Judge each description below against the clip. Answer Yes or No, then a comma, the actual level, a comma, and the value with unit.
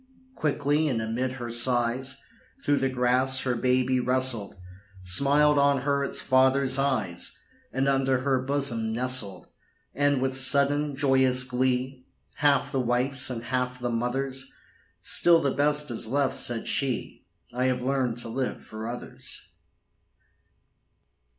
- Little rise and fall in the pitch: Yes, narrow, 1.9 semitones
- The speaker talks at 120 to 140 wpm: Yes, slow, 135 wpm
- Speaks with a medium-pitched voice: No, low, 130 Hz